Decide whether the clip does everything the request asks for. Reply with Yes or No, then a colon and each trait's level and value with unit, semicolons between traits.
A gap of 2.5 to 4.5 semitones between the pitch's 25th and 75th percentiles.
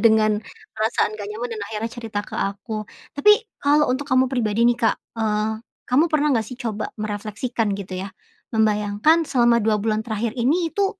Yes: average, 2.9 semitones